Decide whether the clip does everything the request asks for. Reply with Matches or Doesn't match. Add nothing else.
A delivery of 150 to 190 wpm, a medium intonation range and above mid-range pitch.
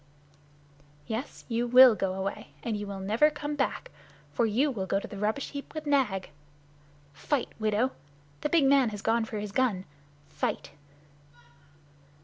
Matches